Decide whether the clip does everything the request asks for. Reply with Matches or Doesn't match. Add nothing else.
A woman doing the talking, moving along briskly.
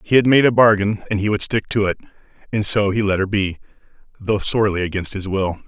Doesn't match